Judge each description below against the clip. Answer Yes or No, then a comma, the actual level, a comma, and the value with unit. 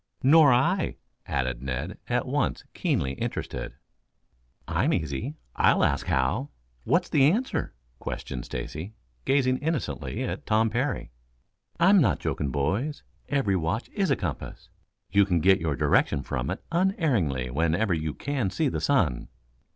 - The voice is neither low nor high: No, low, 100 Hz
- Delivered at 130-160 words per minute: Yes, average, 145 wpm